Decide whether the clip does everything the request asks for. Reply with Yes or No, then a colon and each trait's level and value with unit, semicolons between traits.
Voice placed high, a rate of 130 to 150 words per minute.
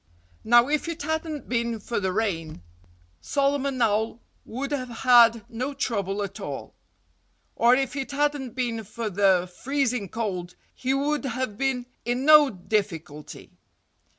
Yes: high, 240 Hz; average, 140 wpm